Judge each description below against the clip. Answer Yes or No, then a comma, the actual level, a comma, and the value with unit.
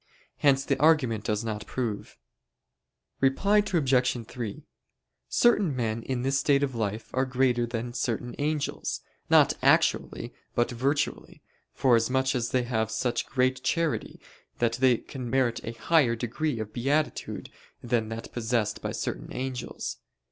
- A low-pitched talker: Yes, low, 125 Hz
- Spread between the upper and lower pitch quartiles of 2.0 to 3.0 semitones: Yes, average, 2.7 semitones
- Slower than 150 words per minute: Yes, average, 140 wpm